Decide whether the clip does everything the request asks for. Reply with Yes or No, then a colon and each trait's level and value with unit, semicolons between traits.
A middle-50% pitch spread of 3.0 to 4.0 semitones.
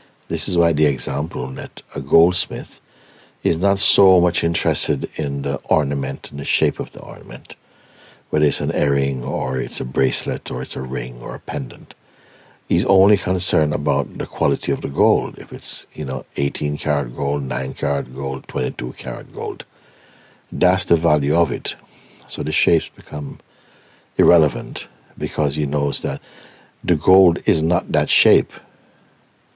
Yes: average, 3.7 semitones